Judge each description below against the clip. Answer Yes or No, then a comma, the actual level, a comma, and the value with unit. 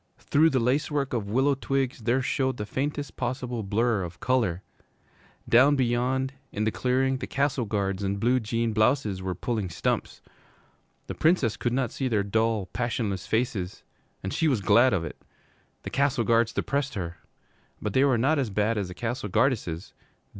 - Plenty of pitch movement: No, average, 4.2 semitones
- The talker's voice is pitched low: Yes, low, 120 Hz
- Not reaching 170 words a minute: No, average, 175 wpm